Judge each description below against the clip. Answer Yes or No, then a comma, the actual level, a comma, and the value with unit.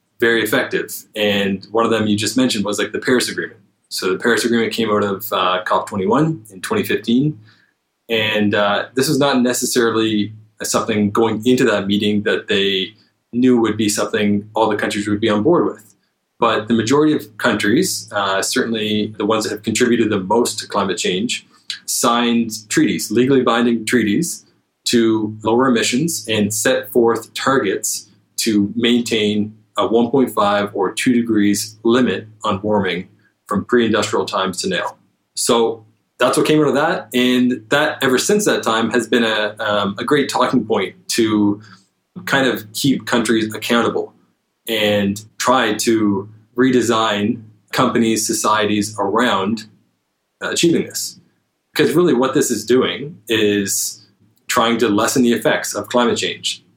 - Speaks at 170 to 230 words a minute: No, average, 155 wpm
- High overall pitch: No, low, 110 Hz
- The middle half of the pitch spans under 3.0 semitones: Yes, narrow, 2.5 semitones